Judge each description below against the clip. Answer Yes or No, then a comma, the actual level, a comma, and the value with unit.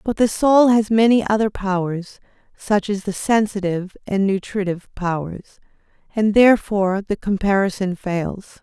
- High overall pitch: Yes, high, 200 Hz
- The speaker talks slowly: Yes, slow, 130 wpm